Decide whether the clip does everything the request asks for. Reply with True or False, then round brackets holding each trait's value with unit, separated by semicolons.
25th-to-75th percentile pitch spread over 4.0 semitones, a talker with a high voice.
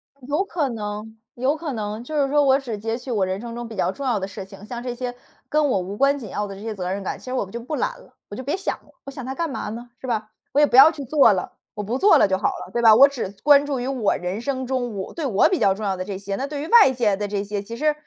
True (5.0 semitones; 240 Hz)